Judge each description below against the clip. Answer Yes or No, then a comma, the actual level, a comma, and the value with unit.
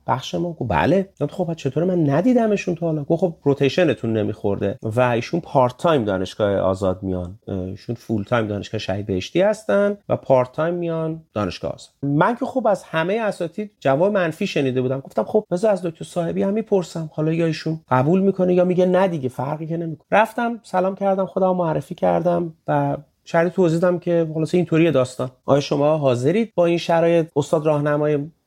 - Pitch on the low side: No, medium, 160 Hz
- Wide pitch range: Yes, wide, 5.7 semitones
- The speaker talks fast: Yes, fast, 185 wpm